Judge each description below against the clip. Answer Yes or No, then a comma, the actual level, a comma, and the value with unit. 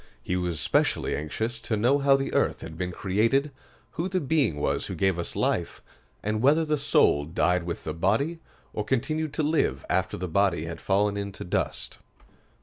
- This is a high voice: No, low, 105 Hz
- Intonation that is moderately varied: No, wide, 7.8 semitones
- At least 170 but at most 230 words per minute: Yes, average, 185 wpm